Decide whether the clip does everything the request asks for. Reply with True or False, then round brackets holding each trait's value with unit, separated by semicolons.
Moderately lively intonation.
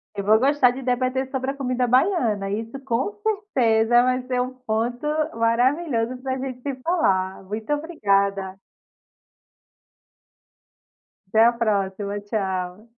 True (3.9 semitones)